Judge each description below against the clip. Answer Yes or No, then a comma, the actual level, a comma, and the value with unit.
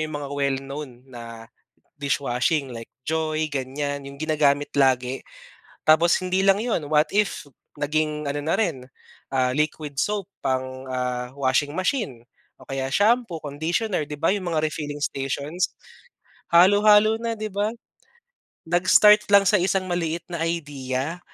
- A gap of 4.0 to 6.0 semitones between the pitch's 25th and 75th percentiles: Yes, average, 4.8 semitones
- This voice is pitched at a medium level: Yes, medium, 150 Hz